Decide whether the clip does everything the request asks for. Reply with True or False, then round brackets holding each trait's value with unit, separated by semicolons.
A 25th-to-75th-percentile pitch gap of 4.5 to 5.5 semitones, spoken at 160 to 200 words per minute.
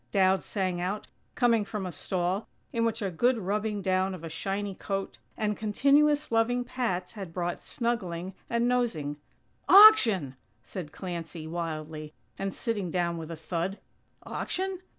False (4.8 semitones; 150 wpm)